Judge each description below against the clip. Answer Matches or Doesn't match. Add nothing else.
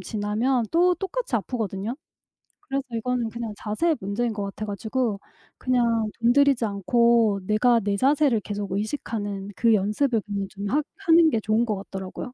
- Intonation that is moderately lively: Matches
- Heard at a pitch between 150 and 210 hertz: Doesn't match